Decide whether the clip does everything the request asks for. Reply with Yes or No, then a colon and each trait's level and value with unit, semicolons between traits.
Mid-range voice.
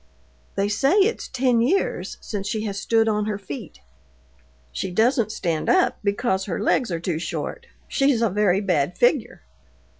No: high, 210 Hz